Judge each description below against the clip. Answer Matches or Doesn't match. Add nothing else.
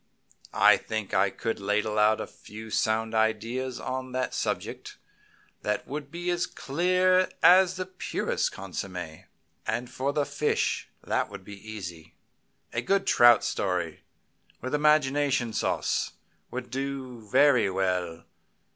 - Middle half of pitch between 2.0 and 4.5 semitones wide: Doesn't match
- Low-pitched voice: Matches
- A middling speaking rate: Doesn't match